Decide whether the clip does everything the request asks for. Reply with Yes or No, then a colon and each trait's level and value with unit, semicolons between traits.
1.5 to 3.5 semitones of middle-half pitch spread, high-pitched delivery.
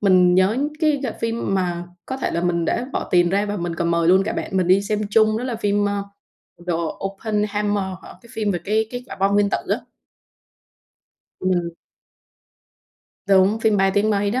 Yes: average, 2.7 semitones; high, 200 Hz